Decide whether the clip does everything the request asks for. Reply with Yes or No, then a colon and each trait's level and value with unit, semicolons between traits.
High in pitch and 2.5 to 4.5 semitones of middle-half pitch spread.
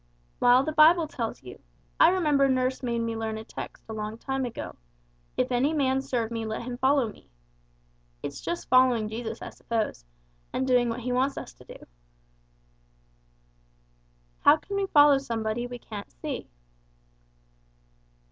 Yes: high, 245 Hz; average, 3.5 semitones